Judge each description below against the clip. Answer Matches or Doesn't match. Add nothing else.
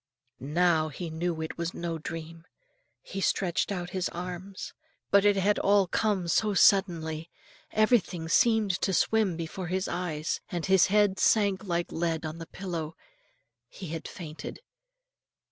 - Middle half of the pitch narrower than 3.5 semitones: Matches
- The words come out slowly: Doesn't match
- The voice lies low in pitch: Doesn't match